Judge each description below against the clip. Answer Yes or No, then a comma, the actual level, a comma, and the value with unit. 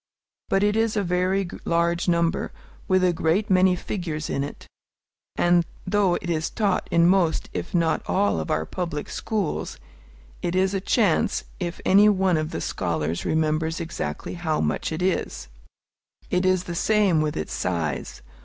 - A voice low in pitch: No, medium, 175 Hz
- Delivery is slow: No, average, 165 wpm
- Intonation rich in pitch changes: No, average, 3.1 semitones